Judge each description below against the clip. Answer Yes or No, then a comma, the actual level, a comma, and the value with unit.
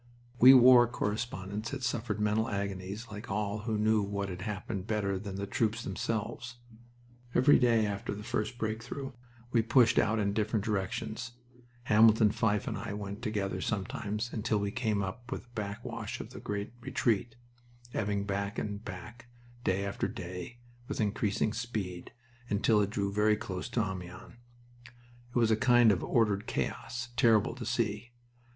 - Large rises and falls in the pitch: No, average, 2.7 semitones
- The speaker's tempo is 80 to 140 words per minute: No, average, 160 wpm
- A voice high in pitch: No, low, 105 Hz